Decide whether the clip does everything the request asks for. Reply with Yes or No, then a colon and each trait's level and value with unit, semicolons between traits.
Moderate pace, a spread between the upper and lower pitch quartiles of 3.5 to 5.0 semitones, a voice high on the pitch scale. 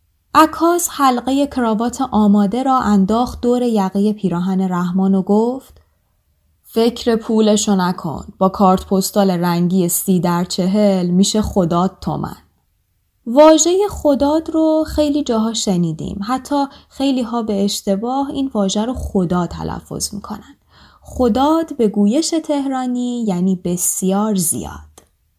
No: average, 120 wpm; wide, 5.6 semitones; high, 210 Hz